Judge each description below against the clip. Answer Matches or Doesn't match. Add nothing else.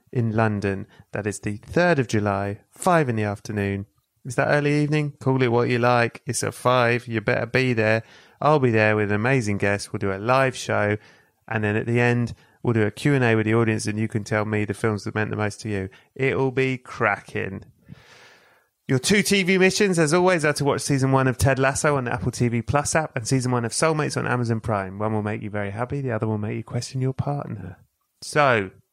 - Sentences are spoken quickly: Matches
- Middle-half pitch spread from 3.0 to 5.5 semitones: Matches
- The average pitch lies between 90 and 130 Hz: Matches